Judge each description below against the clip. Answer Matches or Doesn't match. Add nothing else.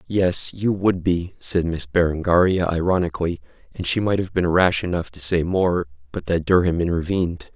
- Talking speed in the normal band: Matches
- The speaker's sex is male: Matches